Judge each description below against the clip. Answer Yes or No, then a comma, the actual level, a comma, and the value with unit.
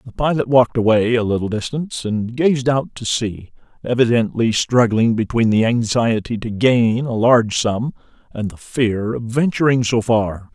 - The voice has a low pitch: Yes, low, 115 Hz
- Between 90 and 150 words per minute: No, average, 165 wpm